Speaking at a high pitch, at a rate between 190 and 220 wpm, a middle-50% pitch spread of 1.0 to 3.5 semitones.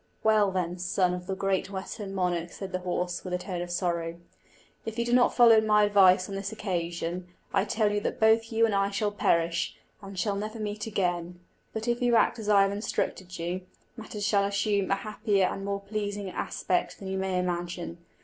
Yes: high, 195 Hz; fast, 205 wpm; average, 2.8 semitones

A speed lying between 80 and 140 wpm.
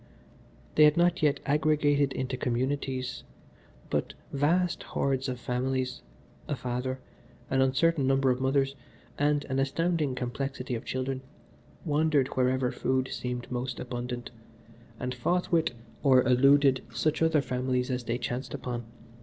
Yes: slow, 135 wpm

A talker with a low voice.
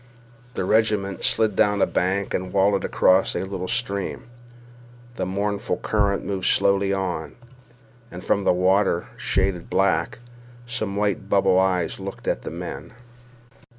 Yes: low, 100 Hz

